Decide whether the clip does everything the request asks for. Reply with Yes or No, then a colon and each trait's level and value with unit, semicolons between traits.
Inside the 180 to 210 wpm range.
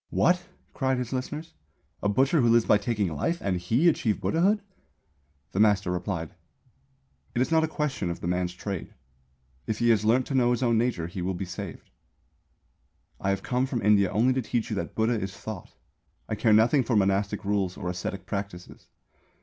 Yes: average, 190 wpm